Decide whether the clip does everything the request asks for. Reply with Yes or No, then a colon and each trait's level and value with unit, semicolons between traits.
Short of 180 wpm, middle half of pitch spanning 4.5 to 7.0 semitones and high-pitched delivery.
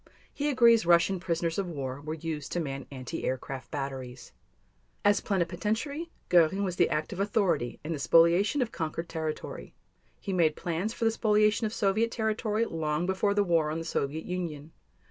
No: average, 170 wpm; average, 5.2 semitones; medium, 175 Hz